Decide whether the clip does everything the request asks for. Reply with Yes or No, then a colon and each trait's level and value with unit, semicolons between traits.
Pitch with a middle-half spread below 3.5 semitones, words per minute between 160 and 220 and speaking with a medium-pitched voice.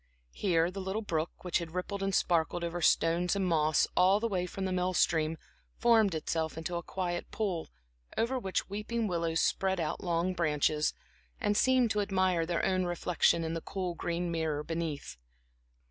Yes: average, 2.7 semitones; average, 175 wpm; medium, 175 Hz